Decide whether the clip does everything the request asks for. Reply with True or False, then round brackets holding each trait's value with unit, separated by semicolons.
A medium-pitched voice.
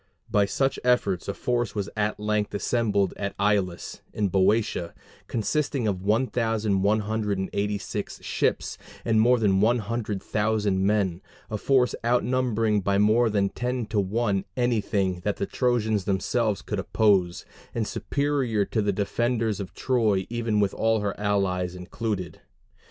False (105 Hz)